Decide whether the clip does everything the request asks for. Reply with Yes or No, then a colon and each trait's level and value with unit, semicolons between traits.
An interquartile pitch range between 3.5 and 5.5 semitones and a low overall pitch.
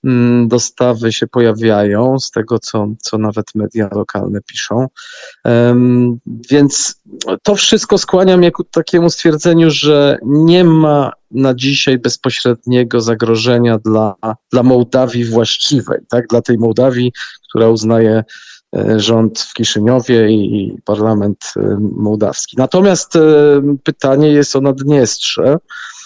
Yes: average, 4.0 semitones; low, 120 Hz